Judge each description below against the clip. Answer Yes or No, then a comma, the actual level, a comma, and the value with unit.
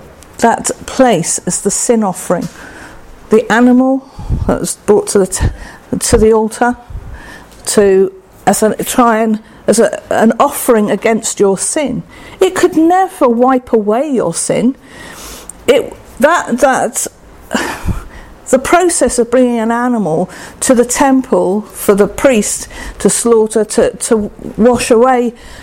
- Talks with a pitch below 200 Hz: No, high, 235 Hz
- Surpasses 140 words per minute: No, slow, 135 wpm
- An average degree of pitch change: Yes, average, 3.8 semitones